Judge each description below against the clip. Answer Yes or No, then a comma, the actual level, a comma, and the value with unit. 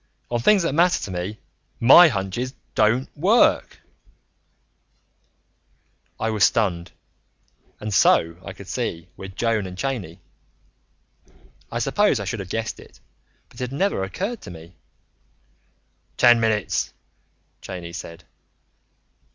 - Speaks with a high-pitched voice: No, low, 110 Hz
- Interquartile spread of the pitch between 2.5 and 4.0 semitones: No, wide, 5.4 semitones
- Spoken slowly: Yes, slow, 125 wpm